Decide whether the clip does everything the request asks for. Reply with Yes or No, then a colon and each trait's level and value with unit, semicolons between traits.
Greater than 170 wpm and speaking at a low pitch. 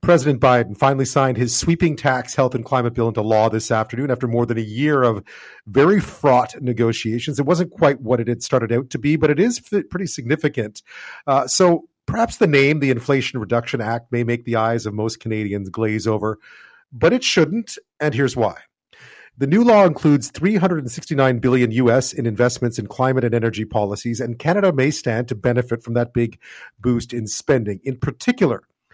Yes: average, 190 wpm; low, 125 Hz